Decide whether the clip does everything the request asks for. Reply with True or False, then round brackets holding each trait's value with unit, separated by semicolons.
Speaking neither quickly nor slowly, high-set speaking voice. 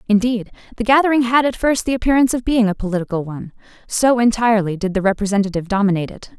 True (190 wpm; 220 Hz)